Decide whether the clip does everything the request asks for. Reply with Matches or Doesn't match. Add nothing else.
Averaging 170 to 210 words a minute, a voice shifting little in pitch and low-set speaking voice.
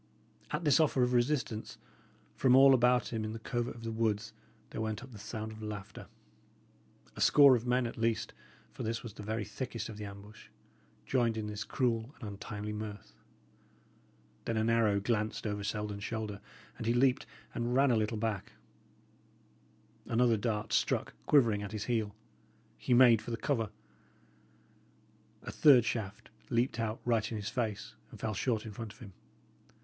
Matches